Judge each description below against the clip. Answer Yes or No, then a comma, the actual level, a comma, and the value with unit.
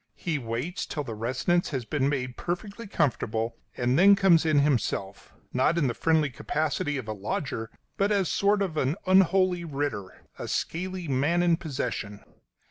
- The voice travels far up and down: Yes, wide, 5.9 semitones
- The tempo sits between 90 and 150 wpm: No, average, 165 wpm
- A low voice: No, medium, 150 Hz